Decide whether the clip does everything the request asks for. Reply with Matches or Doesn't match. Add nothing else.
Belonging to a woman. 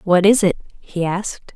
Matches